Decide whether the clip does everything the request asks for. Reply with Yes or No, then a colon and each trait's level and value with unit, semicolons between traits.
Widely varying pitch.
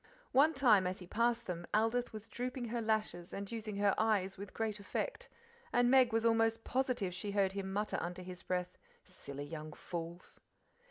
No: average, 4.0 semitones